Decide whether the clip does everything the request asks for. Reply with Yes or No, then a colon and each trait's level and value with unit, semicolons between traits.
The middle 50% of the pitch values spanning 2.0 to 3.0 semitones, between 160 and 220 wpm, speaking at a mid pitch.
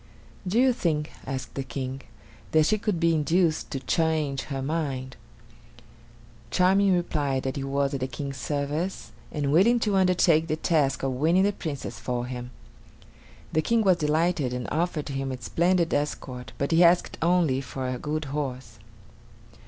No: average, 4.2 semitones; average, 165 wpm; medium, 150 Hz